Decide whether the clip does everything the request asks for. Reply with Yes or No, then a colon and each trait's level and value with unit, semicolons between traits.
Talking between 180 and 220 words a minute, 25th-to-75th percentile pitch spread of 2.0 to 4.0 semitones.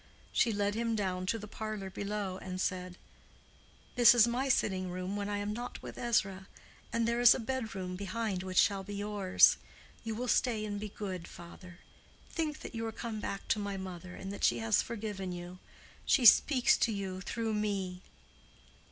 Yes: average, 185 wpm; average, 3.4 semitones